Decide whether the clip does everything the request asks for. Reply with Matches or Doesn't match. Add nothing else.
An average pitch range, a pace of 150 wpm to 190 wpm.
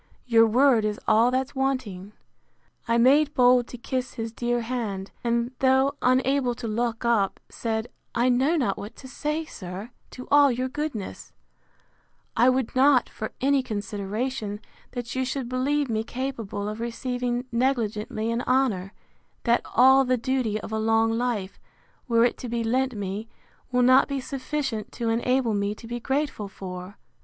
Matches